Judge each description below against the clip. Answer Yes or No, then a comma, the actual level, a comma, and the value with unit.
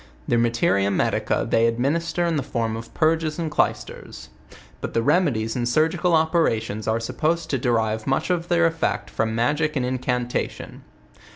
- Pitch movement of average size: No, wide, 5.9 semitones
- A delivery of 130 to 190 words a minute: Yes, average, 170 wpm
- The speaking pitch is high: No, low, 130 Hz